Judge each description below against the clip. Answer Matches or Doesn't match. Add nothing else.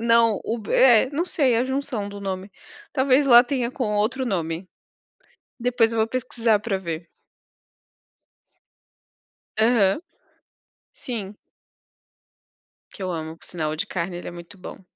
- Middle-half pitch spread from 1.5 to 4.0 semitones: Doesn't match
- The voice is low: Doesn't match